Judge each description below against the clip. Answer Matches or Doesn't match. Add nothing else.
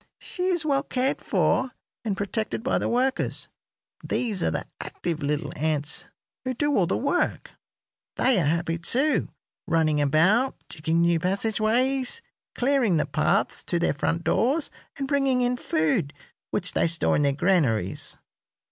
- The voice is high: Matches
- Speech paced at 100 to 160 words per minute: Matches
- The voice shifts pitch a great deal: Matches